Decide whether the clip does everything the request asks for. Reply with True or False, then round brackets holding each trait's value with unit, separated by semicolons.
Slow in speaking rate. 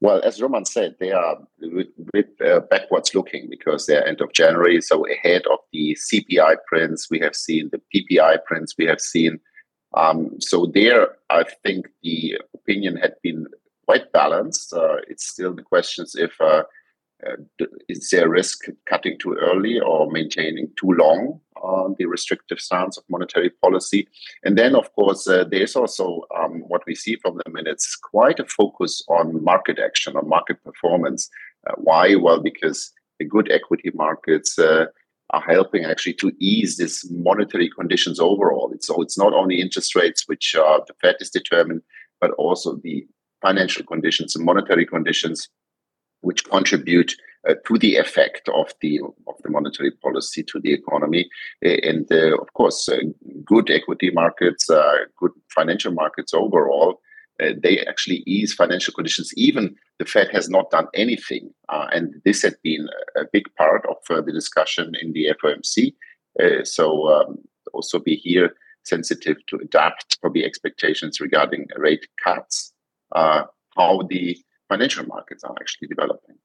False (160 wpm)